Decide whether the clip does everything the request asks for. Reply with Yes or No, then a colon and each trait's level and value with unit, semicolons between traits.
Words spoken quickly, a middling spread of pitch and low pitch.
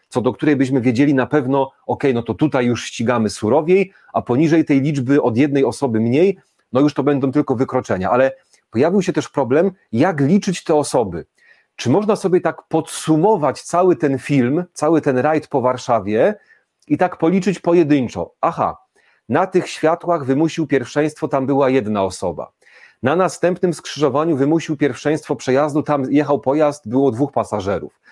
No: fast, 165 wpm; average, 3.6 semitones; medium, 145 Hz